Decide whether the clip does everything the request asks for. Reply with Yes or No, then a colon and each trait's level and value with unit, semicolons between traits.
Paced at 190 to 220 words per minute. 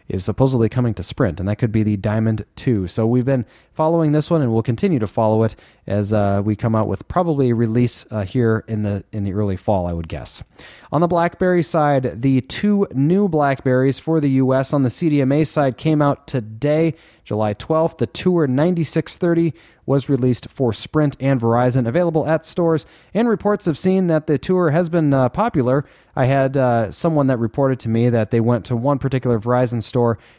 Yes: average, 200 wpm